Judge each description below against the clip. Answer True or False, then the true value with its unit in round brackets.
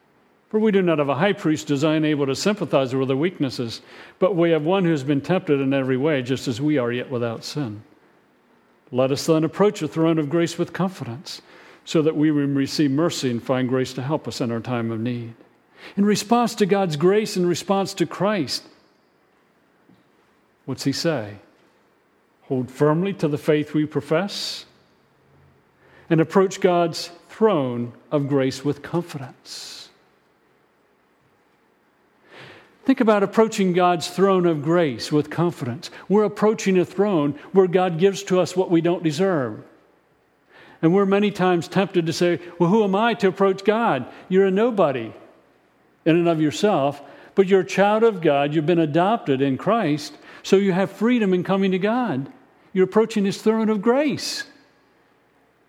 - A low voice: False (170 Hz)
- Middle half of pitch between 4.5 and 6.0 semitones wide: True (5.3 semitones)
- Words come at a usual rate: True (165 wpm)